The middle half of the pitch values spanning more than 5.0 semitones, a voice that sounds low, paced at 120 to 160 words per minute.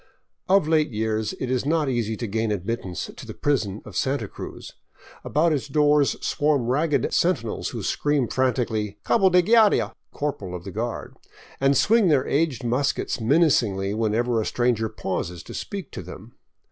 No: wide, 5.4 semitones; low, 125 Hz; average, 170 wpm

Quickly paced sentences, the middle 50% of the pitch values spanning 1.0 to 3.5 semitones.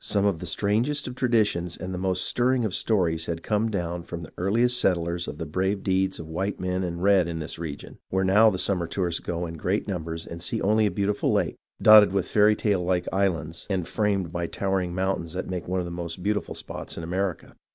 Yes: fast, 225 wpm; average, 3.1 semitones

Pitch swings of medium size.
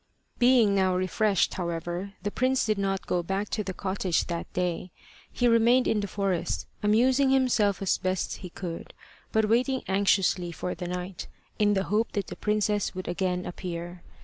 Yes: average, 3.0 semitones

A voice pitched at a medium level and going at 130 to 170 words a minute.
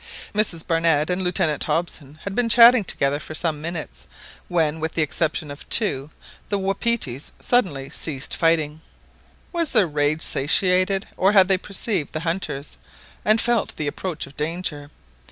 Yes: medium, 165 Hz; average, 155 wpm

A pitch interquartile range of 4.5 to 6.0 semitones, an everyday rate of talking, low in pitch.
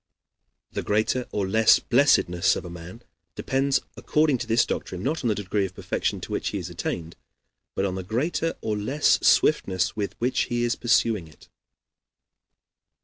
Yes: average, 5.0 semitones; average, 170 wpm; low, 110 Hz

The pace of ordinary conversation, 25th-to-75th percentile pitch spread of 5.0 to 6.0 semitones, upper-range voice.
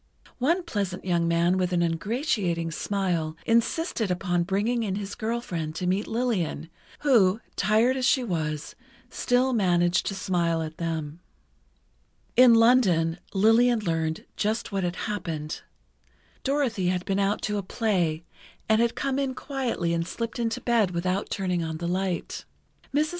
Yes: average, 155 wpm; average, 5.3 semitones; high, 195 Hz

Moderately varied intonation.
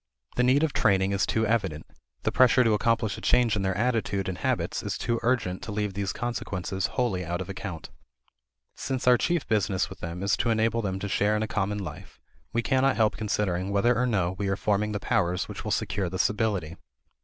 Yes: average, 3.4 semitones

